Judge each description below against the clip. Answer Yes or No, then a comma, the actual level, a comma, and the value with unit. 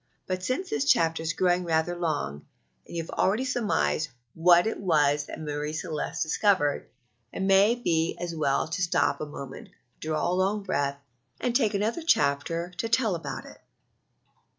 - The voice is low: No, medium, 170 Hz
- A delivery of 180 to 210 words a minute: No, average, 170 wpm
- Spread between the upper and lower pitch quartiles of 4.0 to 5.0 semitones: Yes, average, 4.4 semitones